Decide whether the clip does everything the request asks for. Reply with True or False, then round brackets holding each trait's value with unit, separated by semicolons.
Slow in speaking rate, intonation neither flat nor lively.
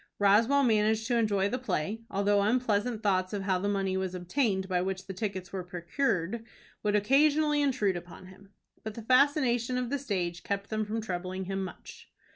False (185 wpm; 4.0 semitones)